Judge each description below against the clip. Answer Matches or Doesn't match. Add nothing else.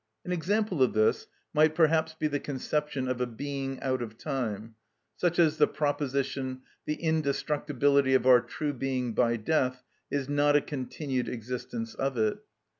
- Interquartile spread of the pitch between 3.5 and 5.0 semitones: Doesn't match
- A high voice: Doesn't match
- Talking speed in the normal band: Matches